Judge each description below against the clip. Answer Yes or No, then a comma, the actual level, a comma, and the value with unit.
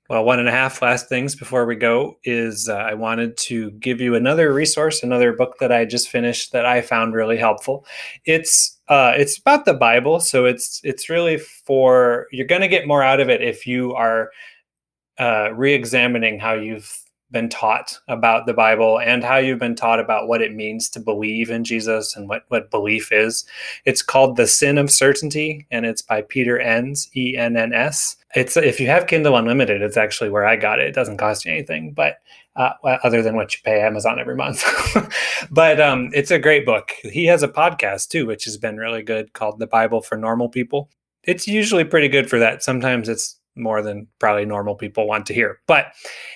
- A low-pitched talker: Yes, low, 120 Hz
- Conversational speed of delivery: No, fast, 210 wpm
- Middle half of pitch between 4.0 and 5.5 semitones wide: No, average, 3.3 semitones